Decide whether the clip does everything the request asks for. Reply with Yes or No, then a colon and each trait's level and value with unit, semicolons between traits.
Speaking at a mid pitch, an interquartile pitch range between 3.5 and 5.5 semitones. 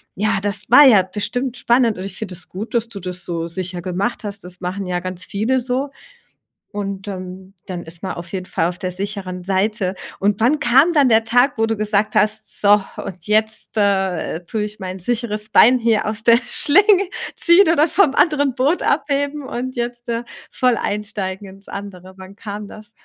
No: high, 210 Hz; average, 4.2 semitones